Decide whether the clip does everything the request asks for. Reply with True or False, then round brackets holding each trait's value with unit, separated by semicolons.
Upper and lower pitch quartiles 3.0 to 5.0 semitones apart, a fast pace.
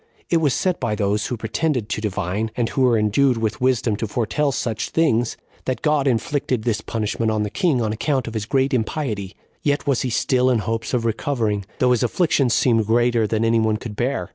True (3.3 semitones; 215 wpm)